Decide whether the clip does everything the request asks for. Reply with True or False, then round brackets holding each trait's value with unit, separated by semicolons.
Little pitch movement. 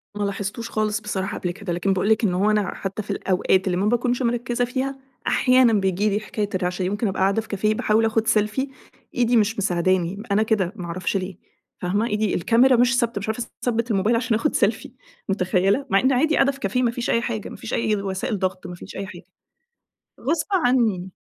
False (3.6 semitones)